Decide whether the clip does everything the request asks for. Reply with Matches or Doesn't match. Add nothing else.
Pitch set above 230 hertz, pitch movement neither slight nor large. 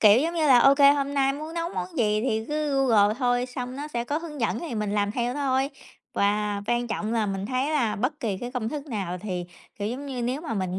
Matches